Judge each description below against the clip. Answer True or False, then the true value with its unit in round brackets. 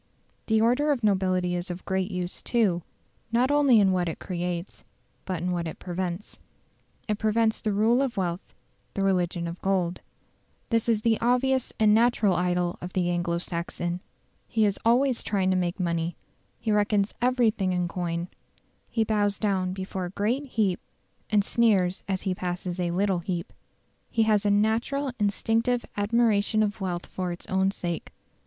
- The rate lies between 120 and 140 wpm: False (170 wpm)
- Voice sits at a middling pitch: False (195 Hz)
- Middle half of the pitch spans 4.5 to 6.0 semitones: False (3.8 semitones)